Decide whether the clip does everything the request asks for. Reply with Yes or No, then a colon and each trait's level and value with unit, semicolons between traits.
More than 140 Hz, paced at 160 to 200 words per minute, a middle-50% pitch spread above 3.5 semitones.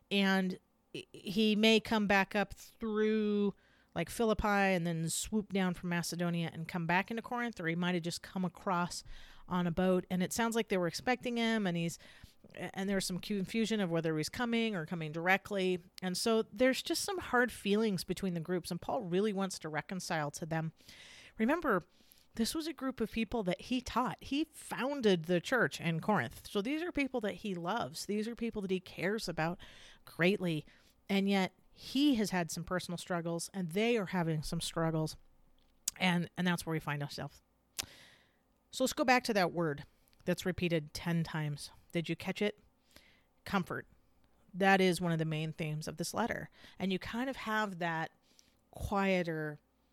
Yes: medium, 185 Hz; average, 185 wpm; average, 4.1 semitones